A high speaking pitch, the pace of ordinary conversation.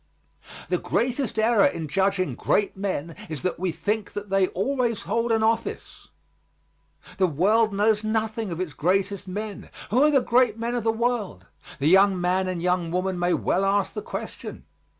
Yes: high, 200 Hz; average, 175 wpm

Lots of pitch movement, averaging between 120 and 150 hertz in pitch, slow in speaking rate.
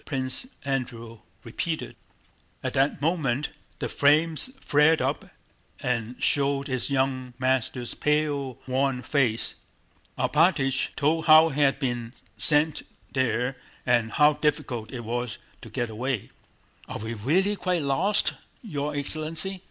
No: average, 3.5 semitones; medium, 140 Hz; slow, 125 wpm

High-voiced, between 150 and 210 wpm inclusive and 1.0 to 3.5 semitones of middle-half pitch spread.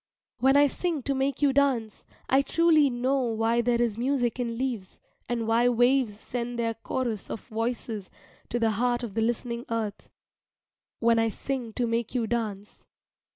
Yes: high, 240 Hz; average, 170 wpm; narrow, 2.4 semitones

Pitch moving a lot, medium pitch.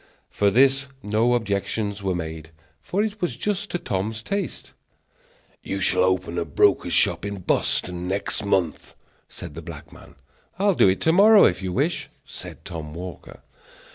No: wide, 7.3 semitones; low, 100 Hz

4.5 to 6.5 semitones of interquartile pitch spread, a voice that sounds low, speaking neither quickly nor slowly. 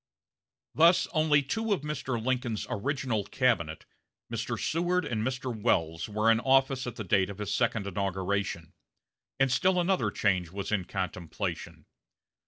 Yes: wide, 5.4 semitones; low, 115 Hz; average, 145 wpm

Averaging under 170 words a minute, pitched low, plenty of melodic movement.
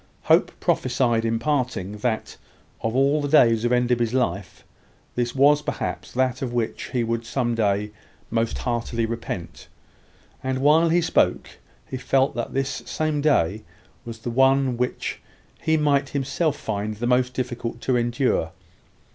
No: average, 150 wpm; low, 125 Hz; average, 2.8 semitones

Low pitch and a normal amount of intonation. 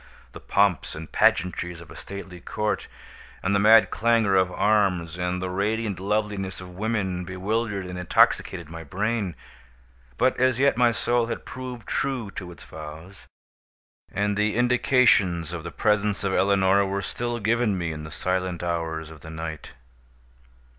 Yes: very low, 95 Hz; average, 3.6 semitones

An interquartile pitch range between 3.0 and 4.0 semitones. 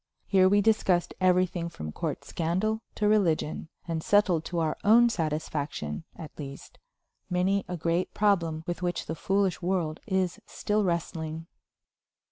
Yes: average, 3.3 semitones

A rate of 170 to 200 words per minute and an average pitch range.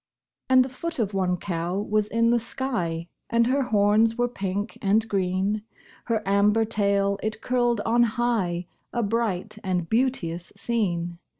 No: average, 155 wpm; average, 3.6 semitones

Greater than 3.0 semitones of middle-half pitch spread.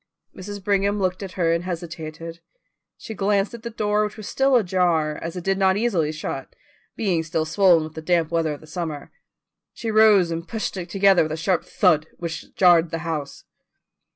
Yes: average, 3.7 semitones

